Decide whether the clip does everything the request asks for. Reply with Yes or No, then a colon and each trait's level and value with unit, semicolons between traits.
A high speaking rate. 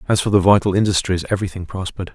No: average, 195 wpm